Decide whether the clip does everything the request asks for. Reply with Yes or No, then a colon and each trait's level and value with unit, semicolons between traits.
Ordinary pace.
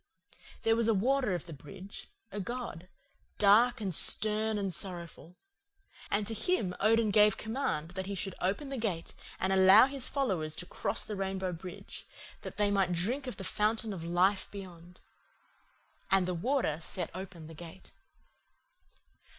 Yes: average, 160 wpm